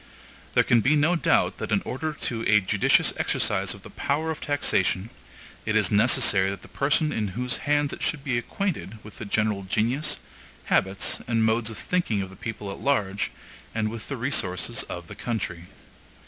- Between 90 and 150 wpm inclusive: No, average, 190 wpm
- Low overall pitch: Yes, low, 110 Hz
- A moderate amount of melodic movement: No, wide, 5.9 semitones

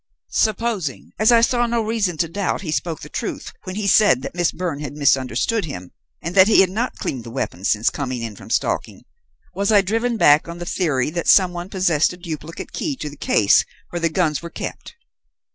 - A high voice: No, medium, 175 Hz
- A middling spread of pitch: No, wide, 5.7 semitones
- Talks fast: Yes, fast, 215 wpm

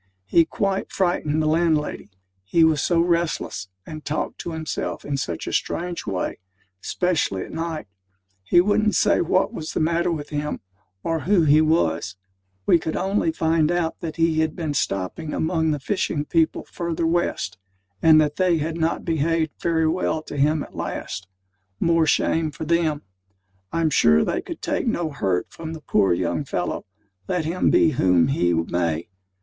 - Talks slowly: No, average, 170 wpm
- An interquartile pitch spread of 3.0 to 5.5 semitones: No, narrow, 2.5 semitones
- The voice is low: No, medium, 160 Hz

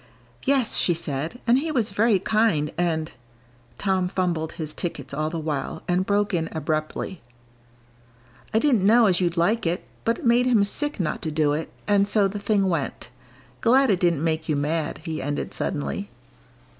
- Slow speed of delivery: No, average, 180 wpm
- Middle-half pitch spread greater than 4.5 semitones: Yes, average, 5.1 semitones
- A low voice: No, medium, 180 Hz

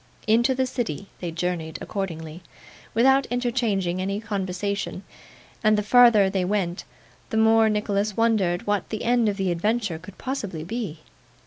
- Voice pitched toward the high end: Yes, high, 205 Hz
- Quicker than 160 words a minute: No, average, 145 wpm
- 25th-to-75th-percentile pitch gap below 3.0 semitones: No, average, 3.9 semitones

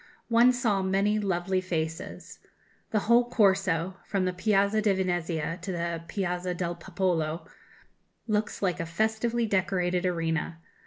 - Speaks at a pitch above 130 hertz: Yes, medium, 185 Hz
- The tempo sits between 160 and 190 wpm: No, slow, 135 wpm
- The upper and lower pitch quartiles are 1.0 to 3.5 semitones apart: Yes, average, 3.1 semitones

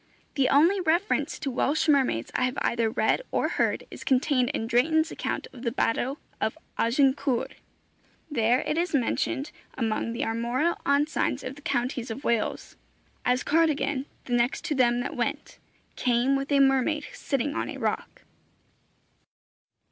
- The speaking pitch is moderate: No, very high, 265 Hz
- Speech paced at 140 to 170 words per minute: Yes, average, 155 wpm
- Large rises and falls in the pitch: No, average, 3.4 semitones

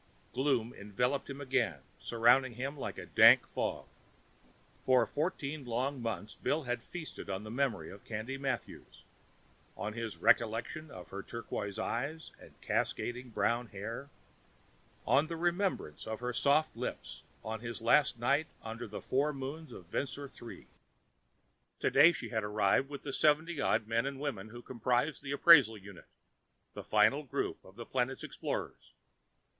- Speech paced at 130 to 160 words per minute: Yes, average, 150 wpm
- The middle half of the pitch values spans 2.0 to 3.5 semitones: No, average, 4.0 semitones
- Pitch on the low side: Yes, low, 125 Hz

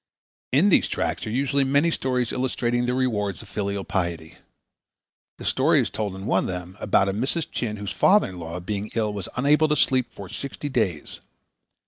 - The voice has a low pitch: Yes, low, 110 Hz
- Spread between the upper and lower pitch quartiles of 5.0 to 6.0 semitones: Yes, average, 5.3 semitones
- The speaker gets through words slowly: No, average, 190 wpm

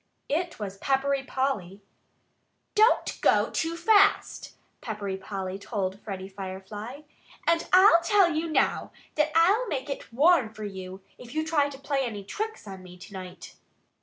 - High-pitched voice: Yes, very high, 260 Hz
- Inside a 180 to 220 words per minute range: No, average, 155 wpm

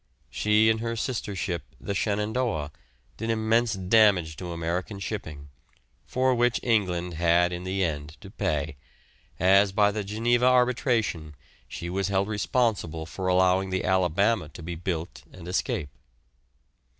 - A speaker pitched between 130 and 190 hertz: No, very low, 95 Hz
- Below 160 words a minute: Yes, average, 140 wpm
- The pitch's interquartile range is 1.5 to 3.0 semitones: No, average, 4.3 semitones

